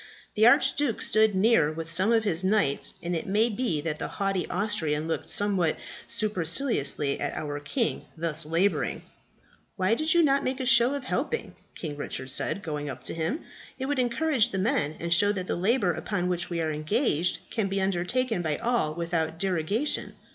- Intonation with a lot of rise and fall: Yes, wide, 6.3 semitones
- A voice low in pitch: No, high, 190 Hz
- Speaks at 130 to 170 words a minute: No, average, 185 wpm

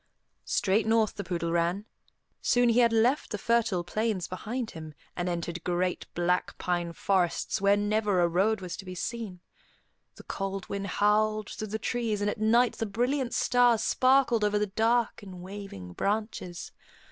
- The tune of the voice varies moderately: Yes, average, 3.8 semitones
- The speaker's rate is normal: Yes, average, 170 wpm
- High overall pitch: Yes, high, 205 Hz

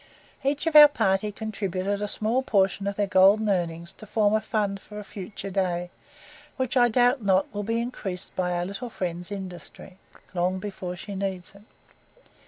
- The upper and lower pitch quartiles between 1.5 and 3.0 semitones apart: Yes, narrow, 2.6 semitones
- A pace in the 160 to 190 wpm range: Yes, average, 180 wpm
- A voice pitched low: No, high, 200 Hz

